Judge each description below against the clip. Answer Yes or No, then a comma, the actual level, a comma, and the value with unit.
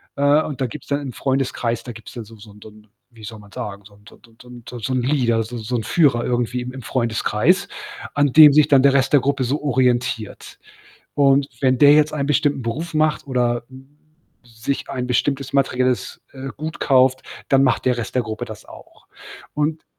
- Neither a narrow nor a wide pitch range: Yes, average, 3.2 semitones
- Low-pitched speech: Yes, low, 130 Hz